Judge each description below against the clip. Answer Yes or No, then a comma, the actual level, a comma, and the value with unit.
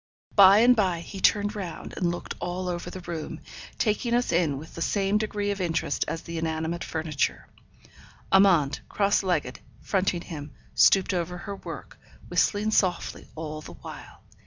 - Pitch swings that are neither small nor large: Yes, average, 3.6 semitones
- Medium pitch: Yes, medium, 180 Hz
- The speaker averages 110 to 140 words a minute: No, average, 165 wpm